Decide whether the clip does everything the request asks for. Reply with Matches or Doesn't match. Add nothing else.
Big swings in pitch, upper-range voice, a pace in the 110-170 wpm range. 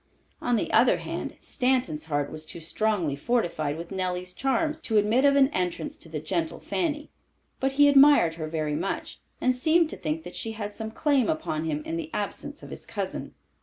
Doesn't match